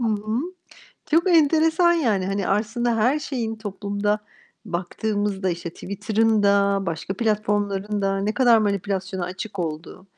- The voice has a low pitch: No, high, 205 Hz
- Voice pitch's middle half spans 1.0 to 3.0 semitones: Yes, narrow, 2.5 semitones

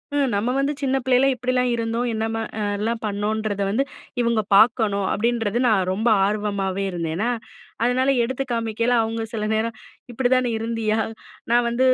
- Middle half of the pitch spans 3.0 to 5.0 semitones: No, narrow, 2.6 semitones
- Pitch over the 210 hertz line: Yes, high, 225 Hz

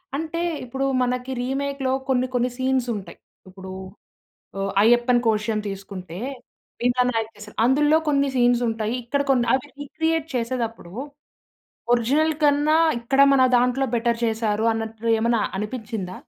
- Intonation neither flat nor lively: Yes, average, 3.3 semitones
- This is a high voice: Yes, high, 240 Hz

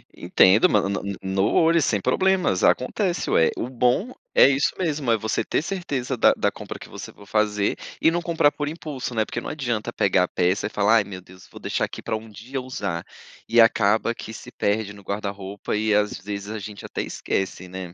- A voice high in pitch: No, low, 110 Hz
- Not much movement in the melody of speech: No, average, 4.7 semitones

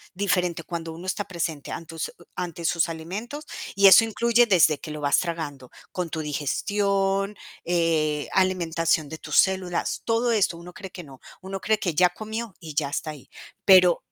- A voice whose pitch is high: No, medium, 175 Hz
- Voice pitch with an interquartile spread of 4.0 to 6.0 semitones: No, average, 3.5 semitones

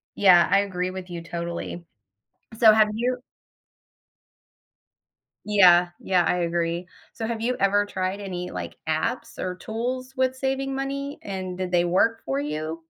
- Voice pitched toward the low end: No, high, 190 Hz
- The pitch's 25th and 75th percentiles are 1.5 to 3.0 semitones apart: No, average, 4.7 semitones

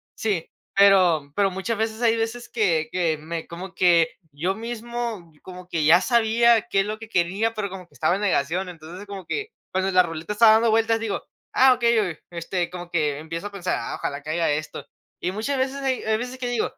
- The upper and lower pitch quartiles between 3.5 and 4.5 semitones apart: No, average, 4.9 semitones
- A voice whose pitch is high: Yes, high, 195 Hz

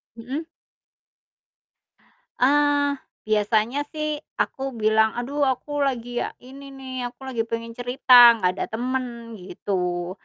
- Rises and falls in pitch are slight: No, average, 3.6 semitones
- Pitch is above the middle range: Yes, high, 245 Hz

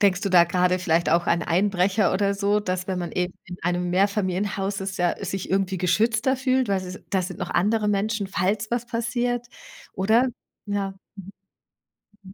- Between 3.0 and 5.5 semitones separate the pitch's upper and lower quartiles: No, narrow, 2.5 semitones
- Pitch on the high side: Yes, high, 195 Hz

